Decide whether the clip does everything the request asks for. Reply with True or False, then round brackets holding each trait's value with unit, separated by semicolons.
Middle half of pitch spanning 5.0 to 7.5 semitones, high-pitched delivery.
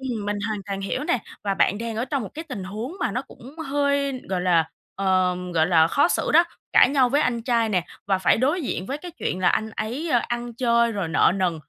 True (5.5 semitones; 230 Hz)